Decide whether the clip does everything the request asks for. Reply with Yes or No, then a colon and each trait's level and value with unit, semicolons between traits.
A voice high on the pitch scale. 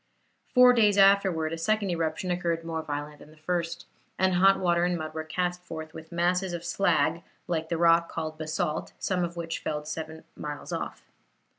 No: medium, 170 Hz